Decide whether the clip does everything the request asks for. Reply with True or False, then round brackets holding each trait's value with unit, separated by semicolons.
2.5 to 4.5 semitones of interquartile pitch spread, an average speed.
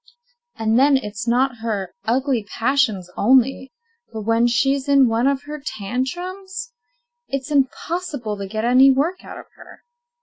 True (3.7 semitones; 145 wpm)